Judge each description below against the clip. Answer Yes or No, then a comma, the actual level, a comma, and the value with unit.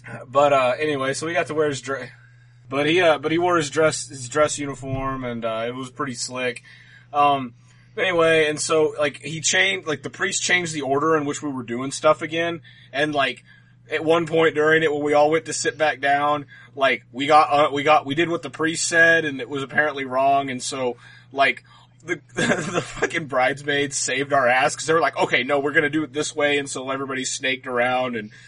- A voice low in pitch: No, medium, 145 Hz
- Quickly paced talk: Yes, fast, 230 wpm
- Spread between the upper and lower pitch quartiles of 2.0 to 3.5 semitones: Yes, average, 3.1 semitones